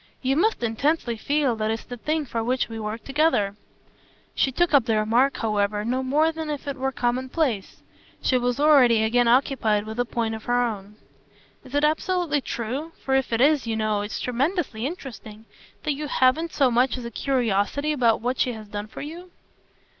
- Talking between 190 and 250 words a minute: Yes, average, 195 wpm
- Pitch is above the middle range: Yes, very high, 250 Hz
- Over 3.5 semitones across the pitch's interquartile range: Yes, average, 4.4 semitones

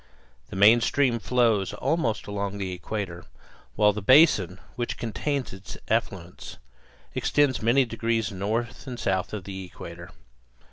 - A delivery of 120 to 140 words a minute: Yes, slow, 135 wpm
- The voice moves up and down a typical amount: Yes, average, 3.8 semitones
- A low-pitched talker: Yes, low, 105 Hz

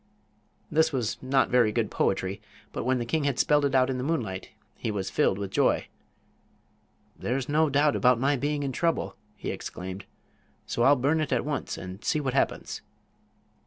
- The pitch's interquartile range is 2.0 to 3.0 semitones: No, average, 5.0 semitones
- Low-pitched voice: Yes, low, 130 Hz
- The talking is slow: No, average, 185 wpm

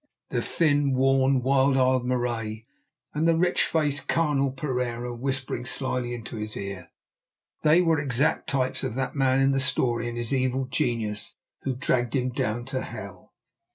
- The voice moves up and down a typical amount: No, narrow, 2.3 semitones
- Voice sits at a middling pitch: No, low, 130 Hz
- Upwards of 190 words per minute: No, average, 160 wpm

